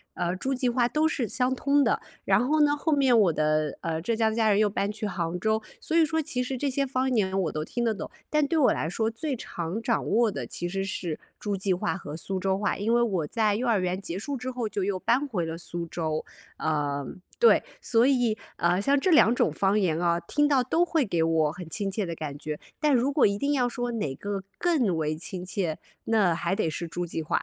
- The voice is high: Yes, high, 205 Hz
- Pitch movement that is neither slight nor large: No, wide, 6.6 semitones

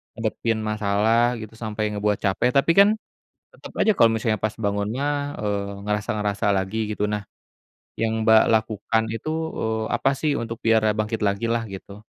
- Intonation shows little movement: Yes, narrow, 1.7 semitones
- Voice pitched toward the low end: Yes, low, 110 Hz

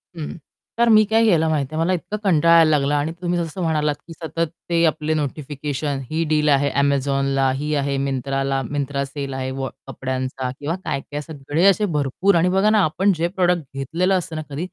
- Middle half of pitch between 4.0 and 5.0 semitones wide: No, average, 3.4 semitones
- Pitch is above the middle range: No, medium, 150 Hz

